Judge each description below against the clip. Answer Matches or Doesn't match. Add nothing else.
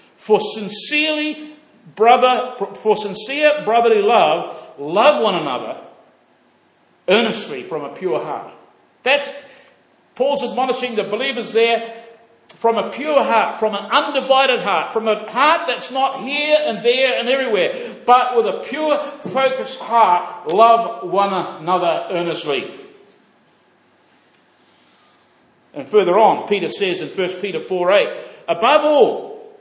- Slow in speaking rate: Matches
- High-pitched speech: Matches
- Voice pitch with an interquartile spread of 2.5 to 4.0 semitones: Doesn't match